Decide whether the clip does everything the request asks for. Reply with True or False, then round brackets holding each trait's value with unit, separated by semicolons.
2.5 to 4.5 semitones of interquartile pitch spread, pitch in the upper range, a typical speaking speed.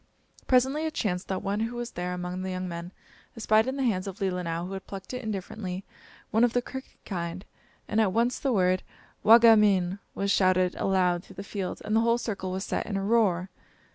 False (3.6 semitones; 195 Hz; 220 wpm)